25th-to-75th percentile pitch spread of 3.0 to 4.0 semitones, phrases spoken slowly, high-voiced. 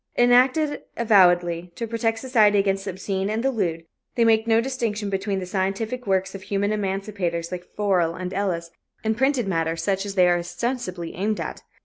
No: average, 3.6 semitones; average, 180 wpm; high, 200 Hz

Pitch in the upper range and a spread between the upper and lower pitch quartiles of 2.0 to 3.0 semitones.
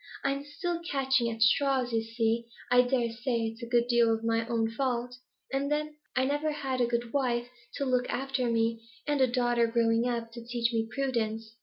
Yes: high, 240 Hz; narrow, 2.6 semitones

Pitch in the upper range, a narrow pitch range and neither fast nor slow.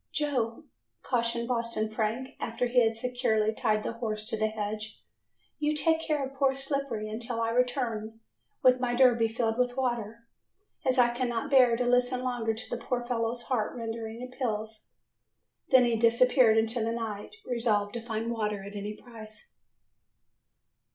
Yes: high, 235 Hz; narrow, 2.2 semitones; average, 160 wpm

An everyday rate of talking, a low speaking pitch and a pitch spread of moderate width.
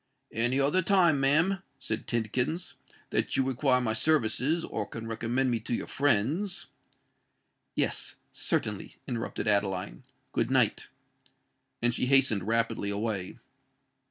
No: slow, 115 wpm; low, 125 Hz; average, 4.4 semitones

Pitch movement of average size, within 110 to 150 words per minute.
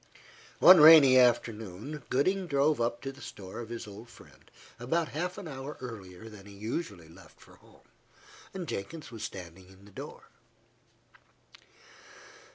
No: wide, 7.0 semitones; average, 145 wpm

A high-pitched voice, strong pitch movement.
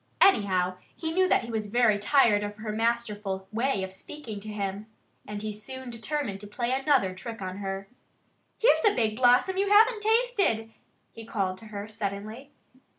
No: high, 220 Hz; average, 4.5 semitones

